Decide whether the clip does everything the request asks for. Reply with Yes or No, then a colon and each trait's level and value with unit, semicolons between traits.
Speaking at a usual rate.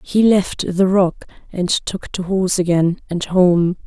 Yes: average, 170 wpm